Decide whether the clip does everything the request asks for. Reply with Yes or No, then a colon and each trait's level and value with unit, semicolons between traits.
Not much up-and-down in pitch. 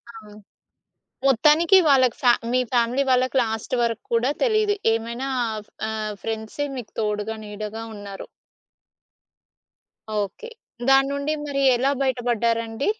No: average, 3.8 semitones